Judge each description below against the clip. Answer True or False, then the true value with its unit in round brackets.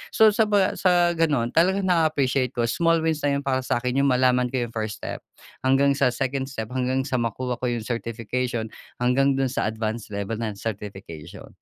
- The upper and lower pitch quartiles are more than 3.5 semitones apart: False (3.2 semitones)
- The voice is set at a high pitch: False (130 Hz)